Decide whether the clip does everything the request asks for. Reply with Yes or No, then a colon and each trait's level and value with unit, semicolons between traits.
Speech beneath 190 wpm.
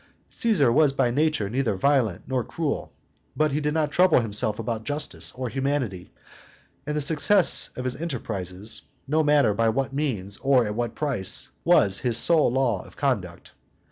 Yes: average, 170 wpm